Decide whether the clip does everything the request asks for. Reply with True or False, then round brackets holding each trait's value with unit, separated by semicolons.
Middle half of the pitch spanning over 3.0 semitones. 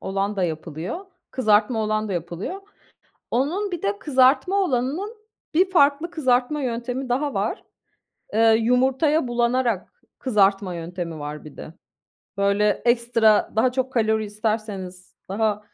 True (4.8 semitones)